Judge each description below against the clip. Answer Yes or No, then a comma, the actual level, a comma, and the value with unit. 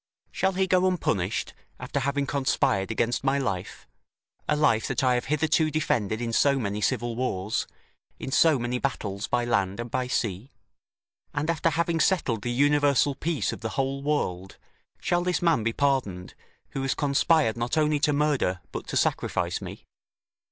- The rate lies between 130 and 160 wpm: No, average, 170 wpm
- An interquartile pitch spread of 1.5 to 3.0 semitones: No, average, 4.9 semitones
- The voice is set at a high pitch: No, low, 135 Hz